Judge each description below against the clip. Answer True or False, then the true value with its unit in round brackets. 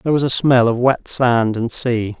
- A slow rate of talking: False (245 wpm)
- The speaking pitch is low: True (120 Hz)